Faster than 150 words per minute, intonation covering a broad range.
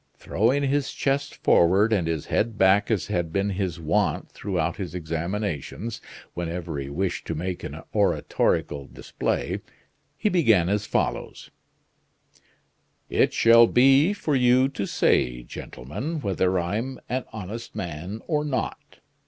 No: slow, 135 wpm; wide, 6.3 semitones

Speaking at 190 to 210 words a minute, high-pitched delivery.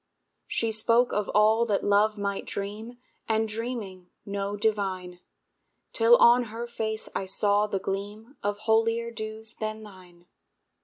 No: average, 140 wpm; high, 215 Hz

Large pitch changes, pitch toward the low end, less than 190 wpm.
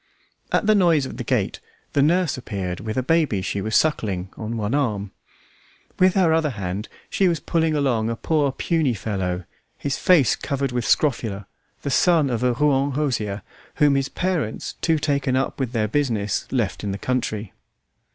Yes: wide, 5.9 semitones; low, 130 Hz; average, 180 wpm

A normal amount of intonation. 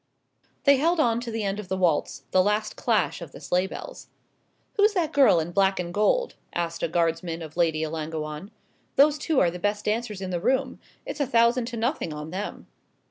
No: wide, 6.7 semitones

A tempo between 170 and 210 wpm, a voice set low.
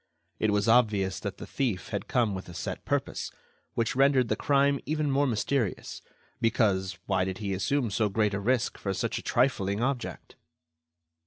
Yes: average, 175 wpm; low, 110 Hz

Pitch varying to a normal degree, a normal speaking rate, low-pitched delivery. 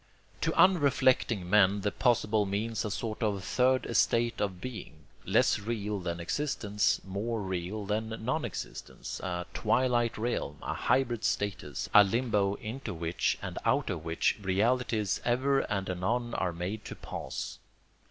Yes: average, 3.8 semitones; average, 145 wpm; low, 105 Hz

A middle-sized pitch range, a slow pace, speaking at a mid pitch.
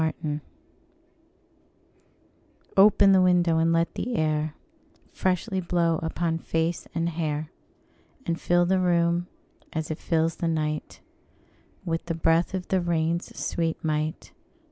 No: narrow, 1.7 semitones; slow, 125 wpm; medium, 165 Hz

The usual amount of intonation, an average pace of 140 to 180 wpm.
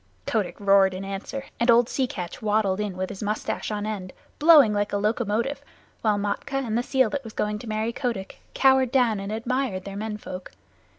No: average, 3.4 semitones; average, 200 wpm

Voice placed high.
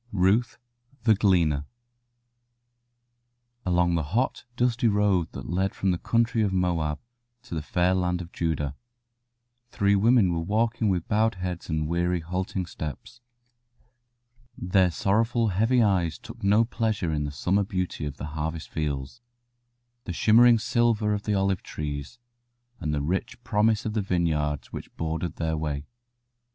No: very low, 90 Hz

